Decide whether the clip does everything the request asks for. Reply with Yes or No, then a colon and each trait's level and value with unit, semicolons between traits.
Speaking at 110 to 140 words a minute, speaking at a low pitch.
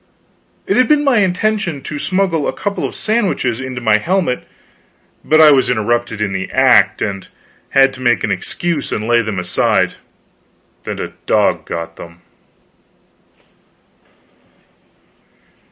Yes: slow, 135 wpm; low, 130 Hz